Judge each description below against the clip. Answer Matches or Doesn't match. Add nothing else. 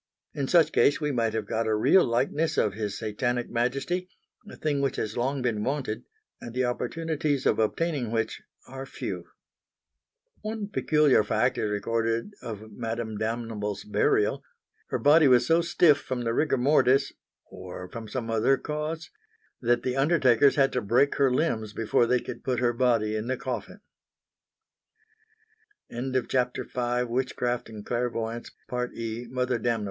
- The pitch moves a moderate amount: Matches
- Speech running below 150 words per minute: Matches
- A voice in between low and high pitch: Doesn't match